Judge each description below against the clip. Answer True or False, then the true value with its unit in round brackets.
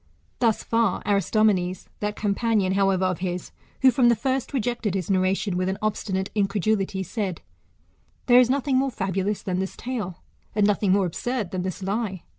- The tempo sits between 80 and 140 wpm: False (180 wpm)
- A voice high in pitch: True (200 Hz)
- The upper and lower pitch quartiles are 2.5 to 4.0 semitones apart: True (3.3 semitones)